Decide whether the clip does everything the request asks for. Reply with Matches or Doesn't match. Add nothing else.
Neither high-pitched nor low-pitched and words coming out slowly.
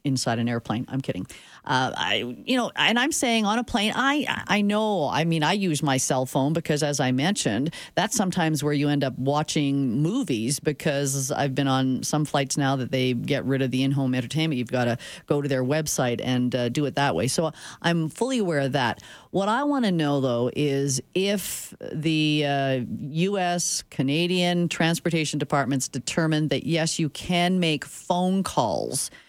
Doesn't match